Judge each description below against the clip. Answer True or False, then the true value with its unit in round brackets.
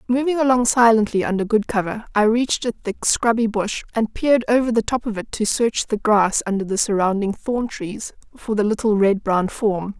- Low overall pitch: False (220 Hz)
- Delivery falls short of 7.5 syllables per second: True (5.2 syllables/s)